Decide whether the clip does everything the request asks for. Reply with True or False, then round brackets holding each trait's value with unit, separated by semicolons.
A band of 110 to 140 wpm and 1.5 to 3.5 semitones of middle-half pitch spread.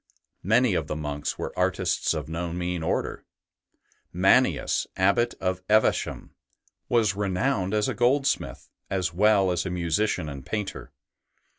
False (135 wpm; 4.1 semitones)